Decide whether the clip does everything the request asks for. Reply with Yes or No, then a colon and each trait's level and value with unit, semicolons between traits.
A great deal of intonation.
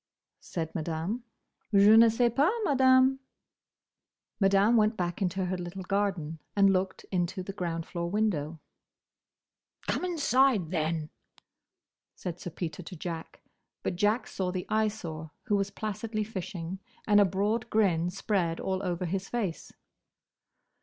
No: average, 3.8 semitones